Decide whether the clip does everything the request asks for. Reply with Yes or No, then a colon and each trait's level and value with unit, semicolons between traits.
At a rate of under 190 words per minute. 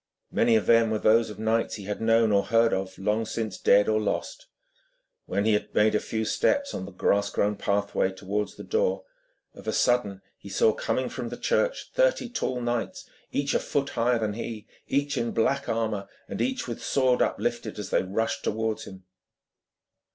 No: average, 195 wpm